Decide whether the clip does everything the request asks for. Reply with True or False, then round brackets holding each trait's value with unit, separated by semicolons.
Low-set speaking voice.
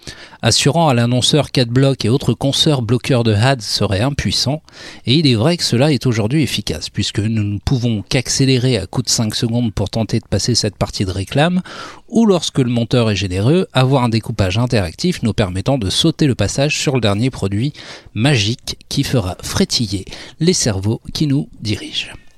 True (120 Hz)